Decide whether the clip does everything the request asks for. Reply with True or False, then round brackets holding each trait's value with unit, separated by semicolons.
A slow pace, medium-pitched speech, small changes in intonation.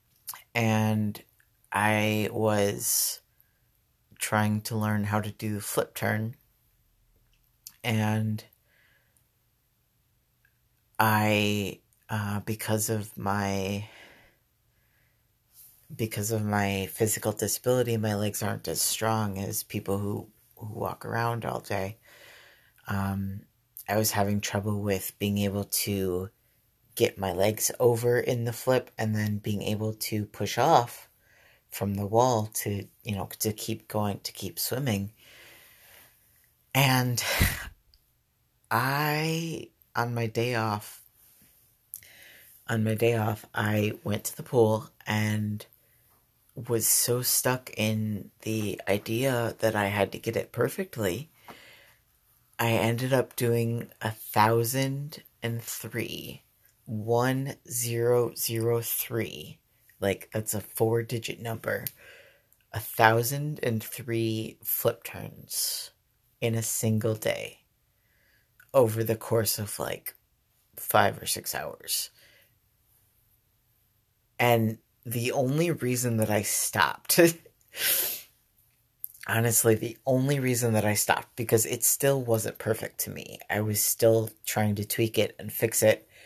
False (115 wpm; 115 Hz; 1.9 semitones)